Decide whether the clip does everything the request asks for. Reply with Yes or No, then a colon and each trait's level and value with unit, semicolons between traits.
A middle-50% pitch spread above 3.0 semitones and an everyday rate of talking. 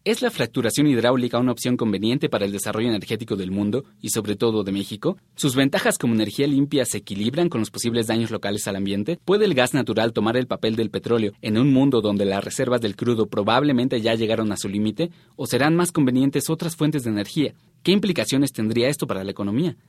No: average, 5.0 semitones; fast, 210 wpm